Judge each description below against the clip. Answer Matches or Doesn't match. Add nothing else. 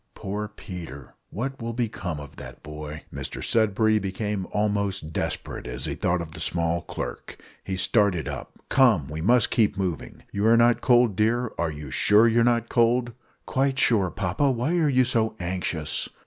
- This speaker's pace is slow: Doesn't match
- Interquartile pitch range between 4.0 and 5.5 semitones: Matches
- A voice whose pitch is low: Matches